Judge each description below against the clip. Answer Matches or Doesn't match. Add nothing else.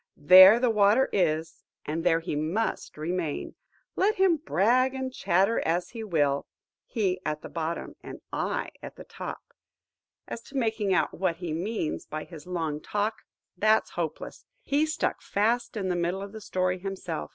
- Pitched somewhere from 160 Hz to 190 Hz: Matches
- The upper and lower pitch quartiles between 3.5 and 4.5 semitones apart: Doesn't match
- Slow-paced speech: Doesn't match